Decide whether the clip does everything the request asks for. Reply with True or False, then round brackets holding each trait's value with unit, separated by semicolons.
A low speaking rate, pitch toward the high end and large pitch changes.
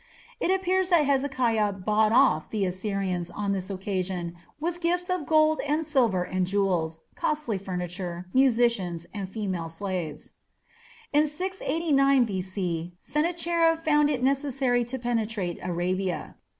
True (125 wpm; 220 Hz; 8.2 semitones)